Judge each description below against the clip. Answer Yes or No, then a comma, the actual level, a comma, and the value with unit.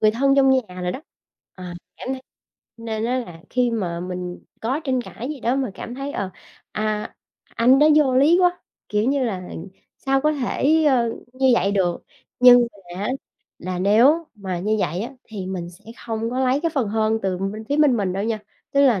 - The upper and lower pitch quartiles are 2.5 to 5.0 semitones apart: No, wide, 5.4 semitones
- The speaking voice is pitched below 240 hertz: Yes, high, 230 Hz